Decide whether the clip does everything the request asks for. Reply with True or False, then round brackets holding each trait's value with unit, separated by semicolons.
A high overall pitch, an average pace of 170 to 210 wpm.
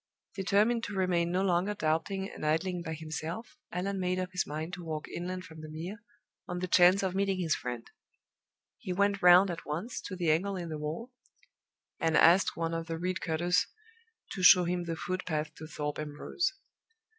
False (180 Hz; 185 wpm)